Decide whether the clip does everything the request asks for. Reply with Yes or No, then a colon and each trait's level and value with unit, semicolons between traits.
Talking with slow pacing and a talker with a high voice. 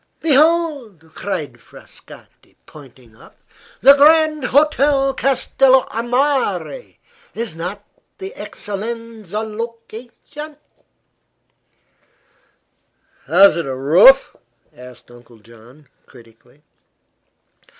Yes: slow, 85 wpm; high, 230 Hz